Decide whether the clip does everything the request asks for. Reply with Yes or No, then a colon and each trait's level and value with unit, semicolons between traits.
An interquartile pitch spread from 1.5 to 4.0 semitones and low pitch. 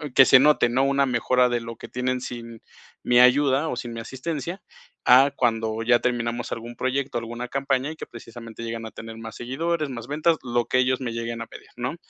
Yes: narrow, 2.6 semitones; low, 125 Hz